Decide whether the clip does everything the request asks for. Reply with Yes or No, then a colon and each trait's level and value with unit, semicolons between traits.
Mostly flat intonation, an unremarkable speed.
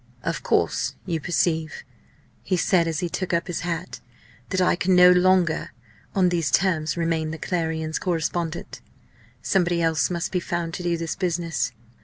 Yes: narrow, 1.8 semitones; average, 165 wpm